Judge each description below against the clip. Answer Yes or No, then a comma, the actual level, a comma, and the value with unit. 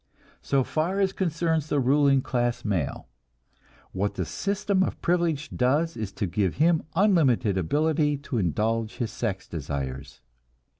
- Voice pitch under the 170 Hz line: Yes, low, 135 Hz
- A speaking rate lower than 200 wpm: Yes, average, 140 wpm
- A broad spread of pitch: Yes, wide, 8.0 semitones